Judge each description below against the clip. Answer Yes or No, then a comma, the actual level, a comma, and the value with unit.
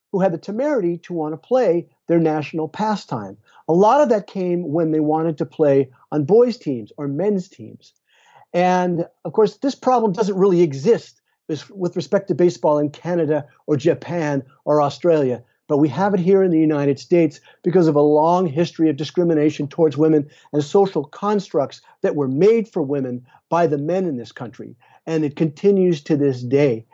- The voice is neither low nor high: Yes, medium, 165 Hz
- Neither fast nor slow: Yes, average, 185 wpm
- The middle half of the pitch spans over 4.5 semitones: No, average, 3.8 semitones